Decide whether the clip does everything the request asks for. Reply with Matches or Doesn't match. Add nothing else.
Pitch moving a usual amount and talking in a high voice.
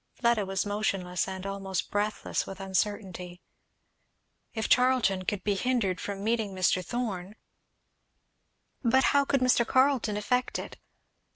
Matches